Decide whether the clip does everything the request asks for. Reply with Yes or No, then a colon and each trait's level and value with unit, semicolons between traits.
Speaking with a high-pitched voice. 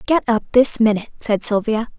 Yes: high, 225 Hz